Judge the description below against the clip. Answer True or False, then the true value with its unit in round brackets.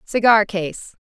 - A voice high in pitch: True (205 Hz)